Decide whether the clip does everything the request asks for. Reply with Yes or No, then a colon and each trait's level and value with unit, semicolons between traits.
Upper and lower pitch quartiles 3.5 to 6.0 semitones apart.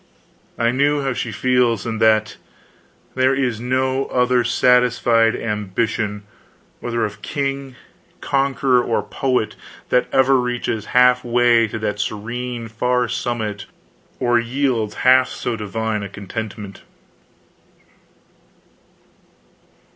No: narrow, 2.4 semitones